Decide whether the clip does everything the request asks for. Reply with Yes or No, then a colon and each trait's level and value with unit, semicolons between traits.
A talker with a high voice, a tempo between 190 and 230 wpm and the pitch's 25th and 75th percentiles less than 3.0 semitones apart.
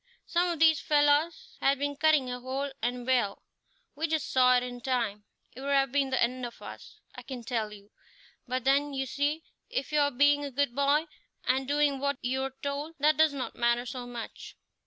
Yes: very high, 270 Hz; fast, 205 wpm; narrow, 2.6 semitones